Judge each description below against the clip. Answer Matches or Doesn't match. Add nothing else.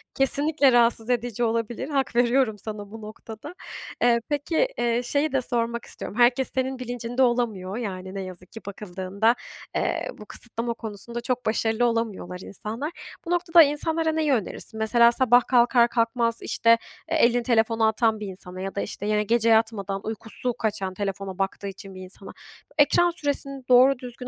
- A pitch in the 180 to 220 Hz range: Doesn't match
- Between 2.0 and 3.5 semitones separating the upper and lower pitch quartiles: Matches